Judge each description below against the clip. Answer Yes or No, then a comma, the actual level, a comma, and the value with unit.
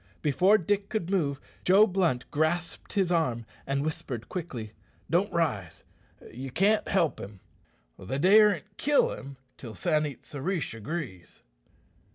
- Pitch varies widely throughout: Yes, wide, 6.3 semitones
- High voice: No, medium, 160 Hz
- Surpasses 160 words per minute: No, average, 140 wpm